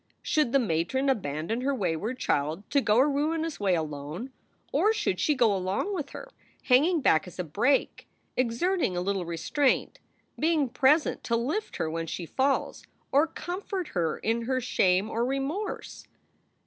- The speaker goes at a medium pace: Yes, average, 160 wpm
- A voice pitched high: Yes, high, 245 Hz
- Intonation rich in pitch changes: Yes, wide, 8.2 semitones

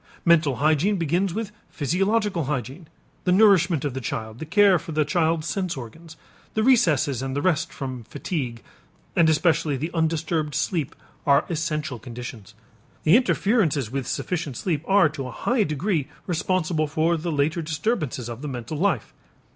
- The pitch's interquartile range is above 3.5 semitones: Yes, average, 4.3 semitones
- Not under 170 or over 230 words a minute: No, average, 160 wpm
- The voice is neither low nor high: Yes, medium, 155 Hz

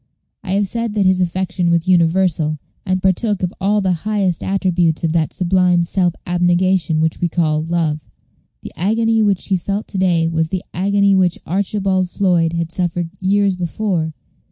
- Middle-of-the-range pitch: Yes, medium, 180 Hz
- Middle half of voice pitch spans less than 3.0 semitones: Yes, narrow, 2.5 semitones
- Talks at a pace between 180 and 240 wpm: No, average, 170 wpm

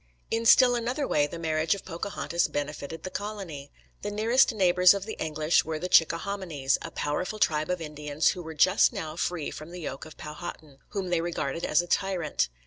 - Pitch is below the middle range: No, medium, 170 Hz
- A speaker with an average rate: Yes, average, 195 wpm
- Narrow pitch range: No, average, 4.4 semitones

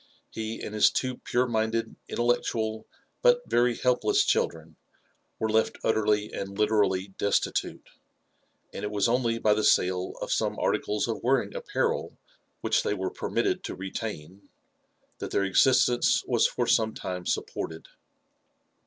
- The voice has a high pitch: No, low, 110 Hz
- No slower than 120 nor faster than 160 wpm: Yes, average, 140 wpm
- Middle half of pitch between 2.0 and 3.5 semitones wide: Yes, average, 3.0 semitones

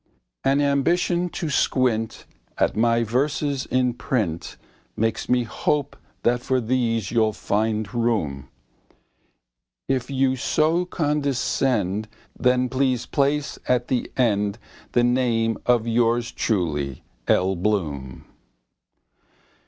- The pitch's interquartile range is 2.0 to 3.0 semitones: No, average, 3.6 semitones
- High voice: No, low, 120 Hz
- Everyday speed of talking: No, slow, 105 wpm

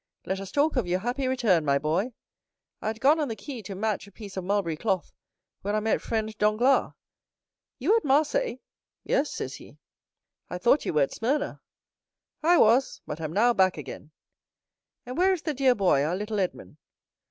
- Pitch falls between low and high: No, high, 220 Hz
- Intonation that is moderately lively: No, wide, 6.2 semitones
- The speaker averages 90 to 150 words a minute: No, average, 185 wpm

